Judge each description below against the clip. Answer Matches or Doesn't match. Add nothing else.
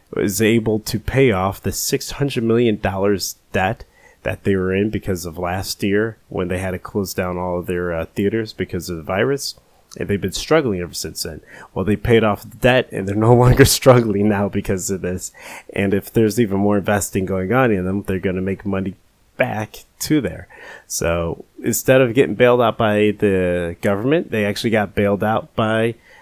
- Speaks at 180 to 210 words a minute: Matches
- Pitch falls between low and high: Doesn't match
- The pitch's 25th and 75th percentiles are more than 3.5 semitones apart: Doesn't match